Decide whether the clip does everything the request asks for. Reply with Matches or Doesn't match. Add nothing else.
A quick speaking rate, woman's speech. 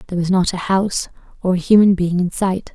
Matches